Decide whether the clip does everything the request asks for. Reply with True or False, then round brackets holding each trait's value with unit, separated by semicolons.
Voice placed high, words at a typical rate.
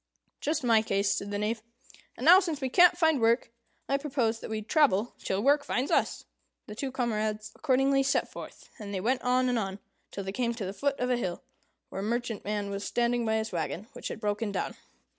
False (230 Hz; 215 wpm)